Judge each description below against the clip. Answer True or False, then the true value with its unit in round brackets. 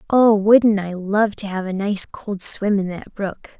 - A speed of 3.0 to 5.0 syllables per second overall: True (3.9 syllables/s)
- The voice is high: True (200 Hz)